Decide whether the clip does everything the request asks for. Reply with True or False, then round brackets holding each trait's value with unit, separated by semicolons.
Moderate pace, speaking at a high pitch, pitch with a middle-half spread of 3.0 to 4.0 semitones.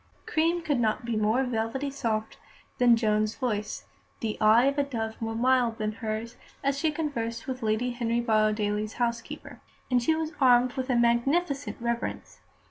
True (165 wpm; 235 Hz; 3.3 semitones)